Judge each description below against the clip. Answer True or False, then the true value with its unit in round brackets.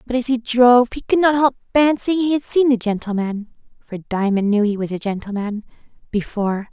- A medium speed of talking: True (180 wpm)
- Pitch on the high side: True (230 Hz)